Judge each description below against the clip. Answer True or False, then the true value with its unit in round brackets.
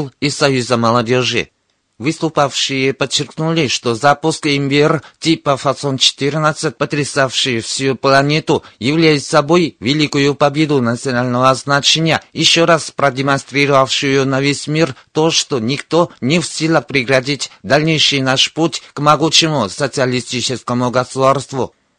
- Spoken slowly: True (105 wpm)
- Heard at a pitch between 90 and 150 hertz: True (140 Hz)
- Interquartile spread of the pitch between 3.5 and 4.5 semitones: False (2.8 semitones)